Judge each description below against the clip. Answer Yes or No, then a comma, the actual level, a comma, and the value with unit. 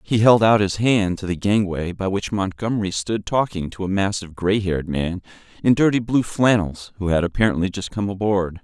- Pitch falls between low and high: No, low, 100 Hz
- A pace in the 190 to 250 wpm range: Yes, average, 200 wpm